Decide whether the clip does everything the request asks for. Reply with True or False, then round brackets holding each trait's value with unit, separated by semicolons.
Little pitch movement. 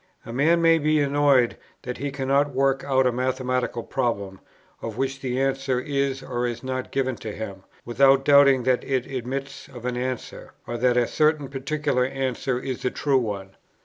True (1.9 semitones)